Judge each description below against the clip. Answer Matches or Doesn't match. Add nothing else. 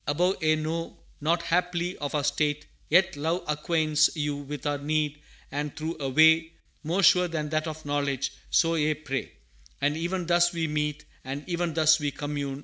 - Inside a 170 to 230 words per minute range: Matches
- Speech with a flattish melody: Matches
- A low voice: Doesn't match